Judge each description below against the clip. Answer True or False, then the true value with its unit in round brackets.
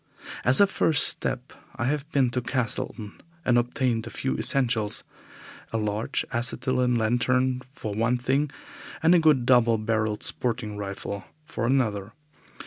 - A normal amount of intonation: True (3.0 semitones)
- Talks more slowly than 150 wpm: True (140 wpm)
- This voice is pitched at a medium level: False (120 Hz)